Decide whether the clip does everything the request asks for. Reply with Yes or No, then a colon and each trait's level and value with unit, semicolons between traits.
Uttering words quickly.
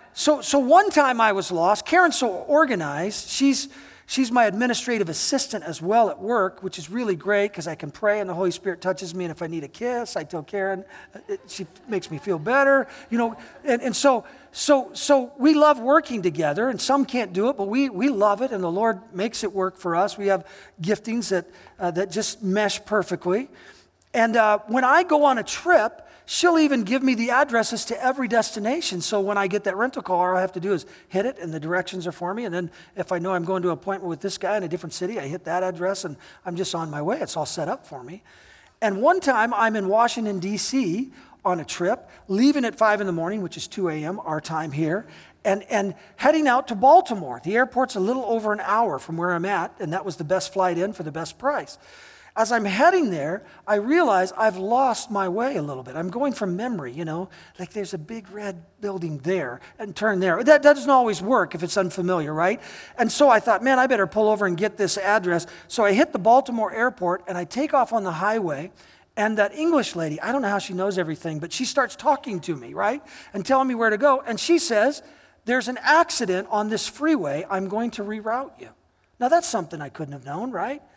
Yes: fast, 235 wpm